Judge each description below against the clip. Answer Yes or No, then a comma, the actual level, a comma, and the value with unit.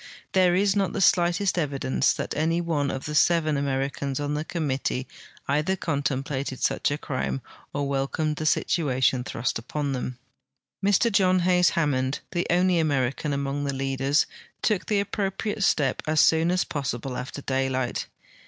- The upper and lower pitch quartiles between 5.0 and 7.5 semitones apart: No, average, 4.4 semitones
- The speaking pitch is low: No, medium, 145 Hz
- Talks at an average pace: Yes, average, 155 wpm